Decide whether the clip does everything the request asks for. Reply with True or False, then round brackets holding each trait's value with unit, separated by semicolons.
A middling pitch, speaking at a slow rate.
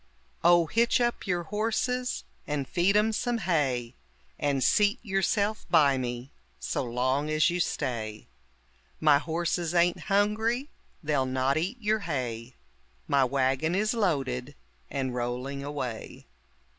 True (155 Hz; 130 wpm)